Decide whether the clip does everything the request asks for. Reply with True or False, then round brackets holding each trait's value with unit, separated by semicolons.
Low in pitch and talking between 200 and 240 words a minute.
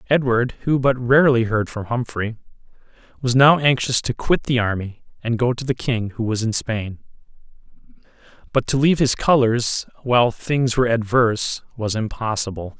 False (120 Hz; 160 wpm)